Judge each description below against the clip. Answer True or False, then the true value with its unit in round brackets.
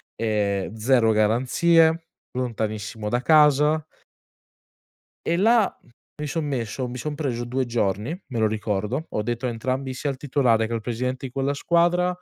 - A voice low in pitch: True (125 Hz)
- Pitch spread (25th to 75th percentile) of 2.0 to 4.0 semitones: False (4.9 semitones)